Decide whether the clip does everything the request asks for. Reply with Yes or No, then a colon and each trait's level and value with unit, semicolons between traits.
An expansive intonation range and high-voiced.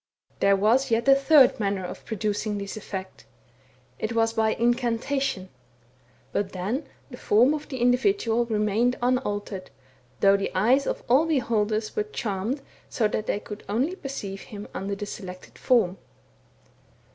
No: average, 4.1 semitones; high, 220 Hz